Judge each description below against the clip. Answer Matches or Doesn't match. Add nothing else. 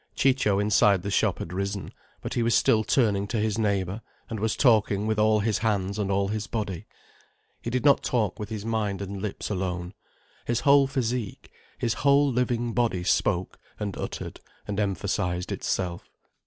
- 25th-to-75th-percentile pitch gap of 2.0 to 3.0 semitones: Matches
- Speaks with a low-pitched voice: Matches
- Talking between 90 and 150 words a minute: Doesn't match